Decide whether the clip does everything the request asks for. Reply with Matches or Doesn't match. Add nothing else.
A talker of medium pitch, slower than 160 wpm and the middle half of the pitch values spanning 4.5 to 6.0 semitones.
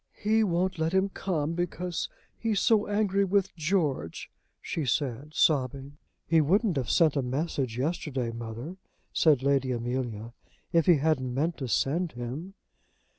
Matches